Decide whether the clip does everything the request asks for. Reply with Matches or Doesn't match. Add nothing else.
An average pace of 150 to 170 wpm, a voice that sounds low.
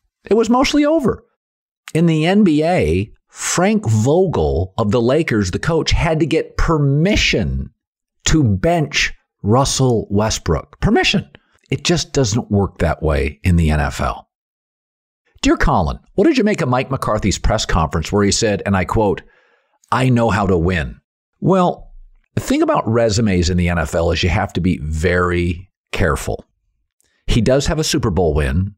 Matches